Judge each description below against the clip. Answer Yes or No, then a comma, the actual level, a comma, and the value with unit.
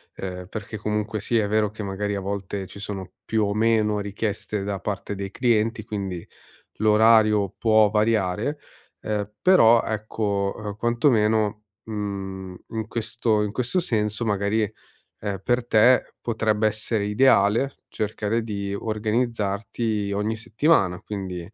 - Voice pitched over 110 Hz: No, low, 105 Hz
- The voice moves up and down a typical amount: No, narrow, 1.8 semitones